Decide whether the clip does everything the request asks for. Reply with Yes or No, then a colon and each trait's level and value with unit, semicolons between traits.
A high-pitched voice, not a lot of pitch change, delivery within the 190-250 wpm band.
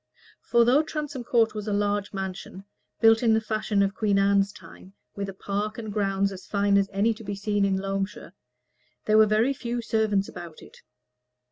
Yes: high, 205 Hz; narrow, 2.0 semitones; average, 195 wpm